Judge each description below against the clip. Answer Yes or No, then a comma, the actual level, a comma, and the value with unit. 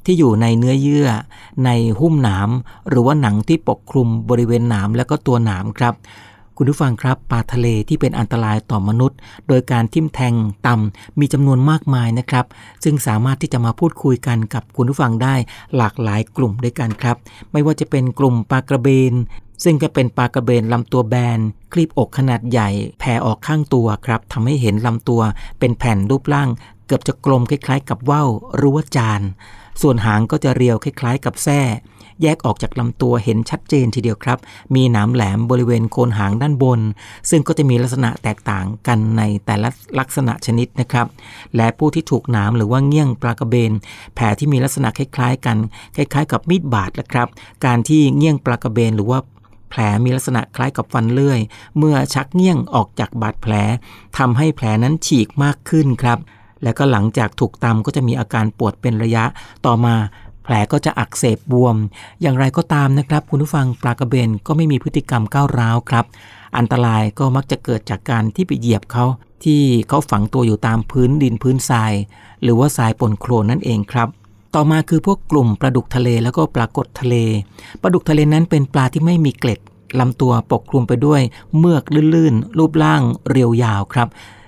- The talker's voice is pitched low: Yes, low, 120 Hz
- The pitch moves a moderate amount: Yes, average, 3.7 semitones